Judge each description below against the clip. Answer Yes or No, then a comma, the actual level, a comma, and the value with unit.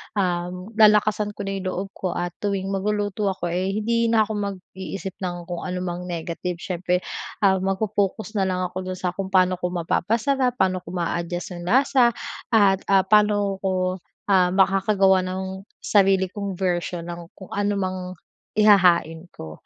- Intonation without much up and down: Yes, narrow, 2.1 semitones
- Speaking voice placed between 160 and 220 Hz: Yes, high, 190 Hz